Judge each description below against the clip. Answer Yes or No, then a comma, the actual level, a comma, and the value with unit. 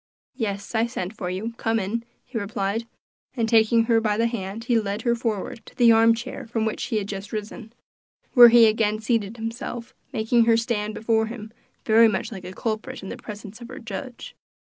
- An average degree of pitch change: No, narrow, 1.8 semitones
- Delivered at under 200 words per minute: No, fast, 205 wpm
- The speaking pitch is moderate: No, high, 225 Hz